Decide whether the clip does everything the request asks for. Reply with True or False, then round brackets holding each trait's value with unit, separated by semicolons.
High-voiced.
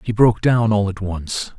False (105 Hz)